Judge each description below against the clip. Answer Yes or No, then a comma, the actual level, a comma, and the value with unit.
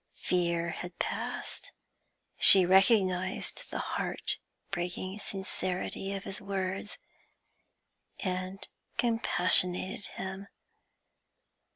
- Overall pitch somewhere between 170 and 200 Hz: Yes, high, 190 Hz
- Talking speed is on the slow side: Yes, slow, 75 wpm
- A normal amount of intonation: No, narrow, 1.3 semitones